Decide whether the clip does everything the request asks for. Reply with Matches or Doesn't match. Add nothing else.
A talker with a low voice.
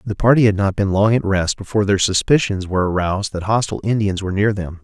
Matches